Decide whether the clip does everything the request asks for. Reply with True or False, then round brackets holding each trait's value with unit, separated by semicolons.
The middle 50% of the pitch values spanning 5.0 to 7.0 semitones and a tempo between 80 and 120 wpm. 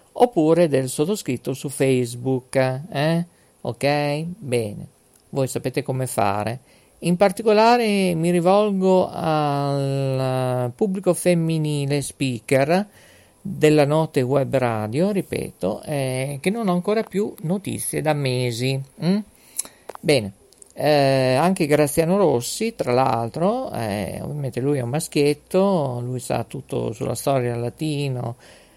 True (5.3 semitones; 115 wpm)